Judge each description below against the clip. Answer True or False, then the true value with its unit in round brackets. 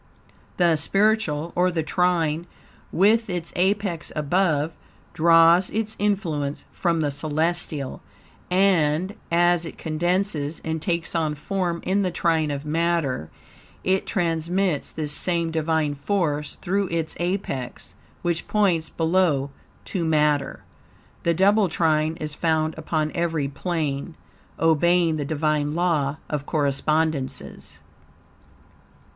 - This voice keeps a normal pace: False (115 wpm)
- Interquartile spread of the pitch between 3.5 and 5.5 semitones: False (2.8 semitones)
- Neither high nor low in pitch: True (165 Hz)